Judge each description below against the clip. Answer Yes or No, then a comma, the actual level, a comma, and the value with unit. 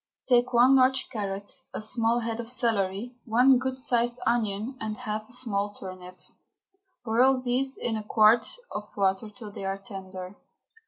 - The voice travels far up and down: No, average, 3.7 semitones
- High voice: Yes, high, 225 Hz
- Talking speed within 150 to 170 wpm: Yes, average, 165 wpm